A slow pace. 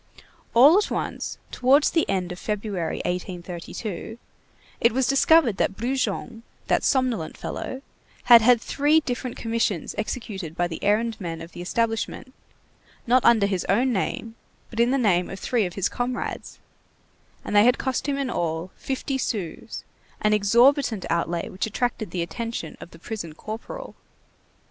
No: average, 155 wpm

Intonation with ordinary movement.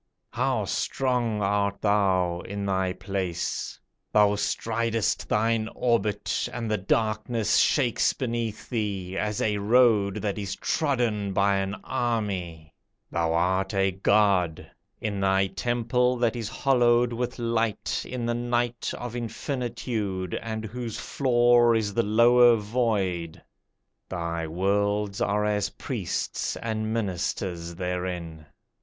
Yes: average, 3.5 semitones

